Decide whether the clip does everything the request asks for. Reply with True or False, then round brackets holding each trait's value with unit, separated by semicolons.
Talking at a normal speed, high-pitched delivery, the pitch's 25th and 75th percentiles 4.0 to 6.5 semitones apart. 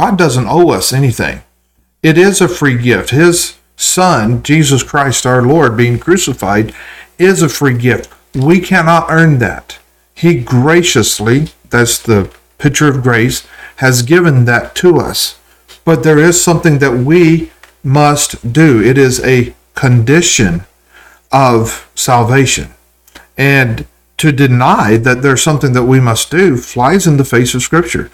False (145 wpm; 135 Hz; 5.2 semitones)